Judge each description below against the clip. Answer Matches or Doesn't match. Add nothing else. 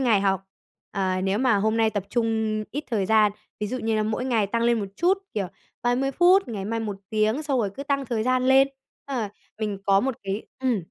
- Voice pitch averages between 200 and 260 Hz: Matches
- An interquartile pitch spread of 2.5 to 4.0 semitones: Matches